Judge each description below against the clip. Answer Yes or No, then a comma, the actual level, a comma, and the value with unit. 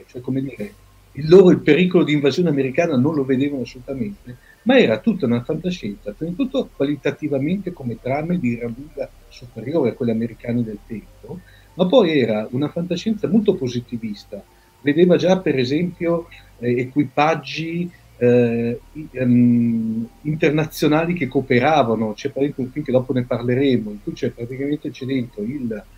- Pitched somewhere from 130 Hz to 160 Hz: Yes, medium, 140 Hz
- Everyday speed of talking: Yes, average, 150 wpm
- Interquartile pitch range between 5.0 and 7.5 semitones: Yes, wide, 5.6 semitones